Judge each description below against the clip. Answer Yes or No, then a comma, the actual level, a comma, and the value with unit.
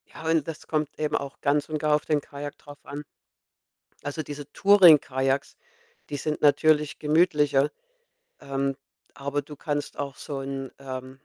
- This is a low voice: No, medium, 145 Hz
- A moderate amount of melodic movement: No, narrow, 1.7 semitones